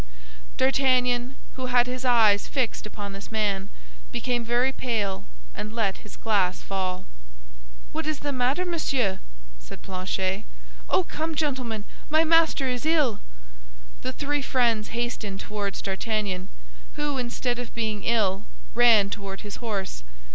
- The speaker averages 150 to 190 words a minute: No, slow, 135 wpm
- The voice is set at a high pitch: Yes, high, 235 Hz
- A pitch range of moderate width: Yes, average, 4.4 semitones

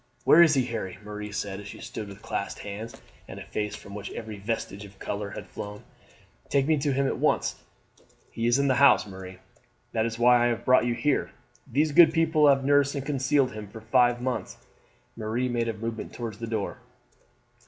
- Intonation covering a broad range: No, average, 4.4 semitones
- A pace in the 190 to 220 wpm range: Yes, fast, 205 wpm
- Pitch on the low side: Yes, low, 115 Hz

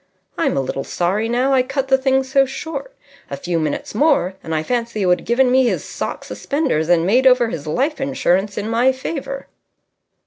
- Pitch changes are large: Yes, wide, 6.9 semitones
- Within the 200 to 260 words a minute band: Yes, fast, 205 wpm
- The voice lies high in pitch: Yes, high, 245 Hz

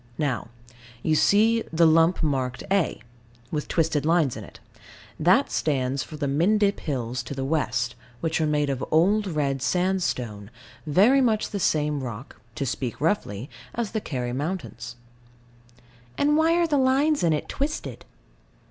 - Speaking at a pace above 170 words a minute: No, average, 155 wpm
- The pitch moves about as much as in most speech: No, wide, 6.9 semitones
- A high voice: No, medium, 155 Hz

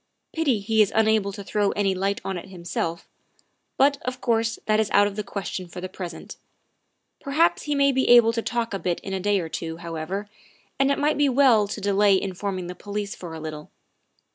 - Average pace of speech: No, fast, 215 wpm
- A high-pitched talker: Yes, high, 205 Hz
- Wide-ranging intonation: No, average, 3.7 semitones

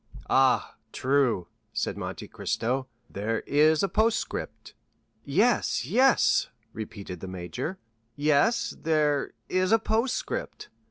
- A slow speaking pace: Yes, slow, 85 wpm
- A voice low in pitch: No, medium, 145 Hz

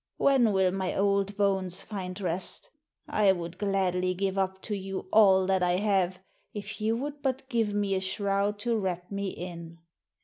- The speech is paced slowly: No, average, 175 wpm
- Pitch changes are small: Yes, narrow, 1.9 semitones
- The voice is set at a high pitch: Yes, high, 195 Hz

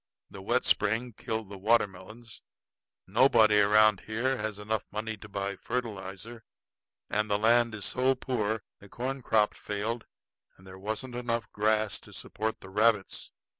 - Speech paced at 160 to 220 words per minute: No, average, 145 wpm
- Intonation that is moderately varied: No, narrow, 2.3 semitones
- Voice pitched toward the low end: Yes, low, 110 Hz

